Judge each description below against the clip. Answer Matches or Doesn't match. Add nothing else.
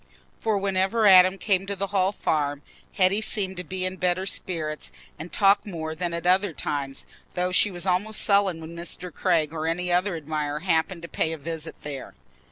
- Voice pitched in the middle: Matches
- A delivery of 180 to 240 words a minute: Matches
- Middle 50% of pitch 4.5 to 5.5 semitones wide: Doesn't match